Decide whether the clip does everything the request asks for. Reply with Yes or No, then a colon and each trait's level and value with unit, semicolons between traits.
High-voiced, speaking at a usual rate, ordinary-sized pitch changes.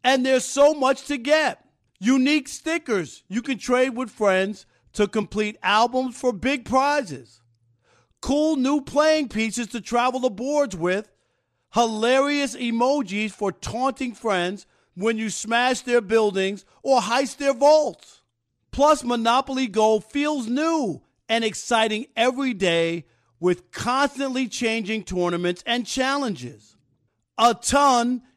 No: high, 240 Hz; slow, 125 wpm; average, 4.9 semitones